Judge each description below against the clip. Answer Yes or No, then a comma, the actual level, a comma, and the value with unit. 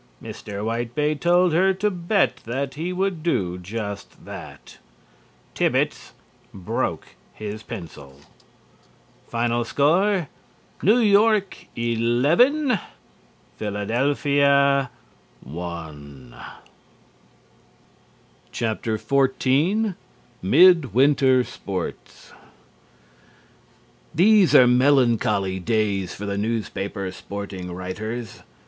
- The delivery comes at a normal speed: No, slow, 75 wpm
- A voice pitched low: Yes, low, 120 Hz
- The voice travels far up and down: Yes, wide, 8.5 semitones